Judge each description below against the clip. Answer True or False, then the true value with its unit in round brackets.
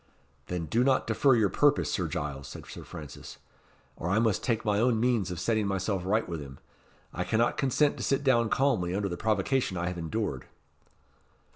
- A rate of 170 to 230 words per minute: True (190 wpm)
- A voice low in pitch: True (105 Hz)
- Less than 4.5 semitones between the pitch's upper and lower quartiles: False (5.1 semitones)